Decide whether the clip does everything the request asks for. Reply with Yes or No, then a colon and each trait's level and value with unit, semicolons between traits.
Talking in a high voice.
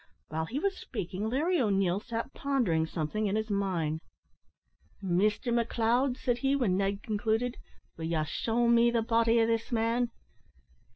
Yes: high, 225 Hz